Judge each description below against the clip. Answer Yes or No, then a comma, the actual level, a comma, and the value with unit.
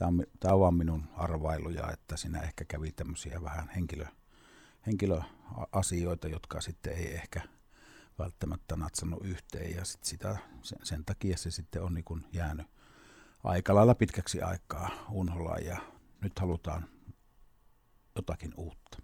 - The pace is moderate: Yes, average, 125 wpm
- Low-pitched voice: Yes, very low, 85 Hz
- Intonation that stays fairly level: Yes, narrow, 2.3 semitones